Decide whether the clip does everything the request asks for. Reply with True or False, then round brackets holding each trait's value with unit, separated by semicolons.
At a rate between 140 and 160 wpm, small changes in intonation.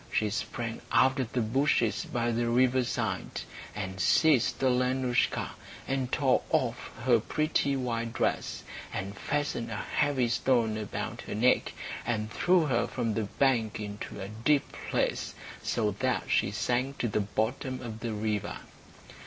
False (145 wpm; 3.1 semitones)